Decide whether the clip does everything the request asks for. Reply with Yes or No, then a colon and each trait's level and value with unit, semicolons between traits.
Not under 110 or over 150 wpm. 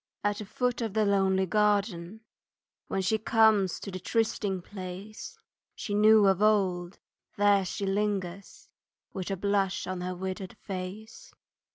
Yes: average, 145 wpm